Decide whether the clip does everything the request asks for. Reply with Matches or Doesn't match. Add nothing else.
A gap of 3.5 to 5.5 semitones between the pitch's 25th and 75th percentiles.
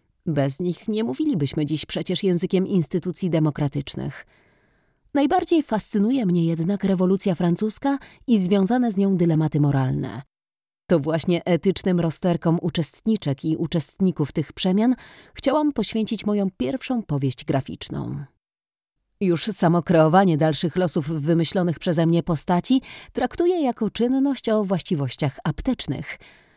Matches